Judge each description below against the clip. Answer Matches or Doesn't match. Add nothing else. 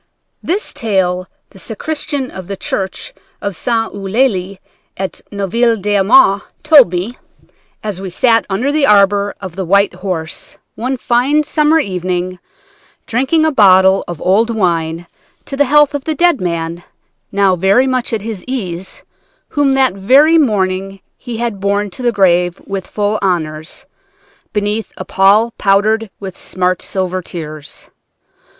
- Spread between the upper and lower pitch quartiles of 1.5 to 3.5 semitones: Doesn't match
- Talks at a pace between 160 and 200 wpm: Doesn't match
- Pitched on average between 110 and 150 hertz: Doesn't match